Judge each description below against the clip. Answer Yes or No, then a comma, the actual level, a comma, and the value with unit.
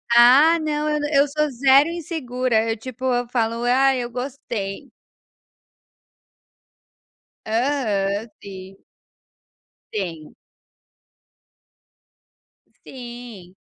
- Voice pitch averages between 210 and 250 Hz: Yes, high, 245 Hz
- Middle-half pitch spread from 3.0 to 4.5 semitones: Yes, average, 4.0 semitones